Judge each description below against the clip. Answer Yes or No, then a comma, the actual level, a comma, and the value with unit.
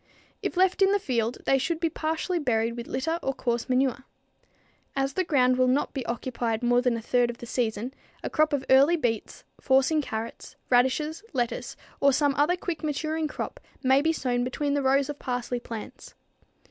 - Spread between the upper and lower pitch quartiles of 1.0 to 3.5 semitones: No, average, 3.9 semitones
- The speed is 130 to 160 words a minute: No, average, 195 wpm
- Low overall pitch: No, very high, 265 Hz